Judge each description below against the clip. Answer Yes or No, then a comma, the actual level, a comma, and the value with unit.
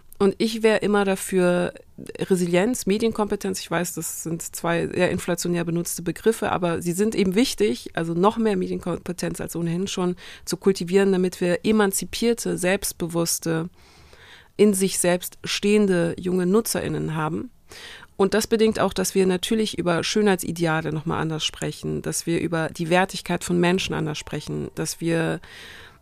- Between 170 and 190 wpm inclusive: No, average, 150 wpm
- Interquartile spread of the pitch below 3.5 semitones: Yes, average, 2.8 semitones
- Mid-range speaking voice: Yes, medium, 180 Hz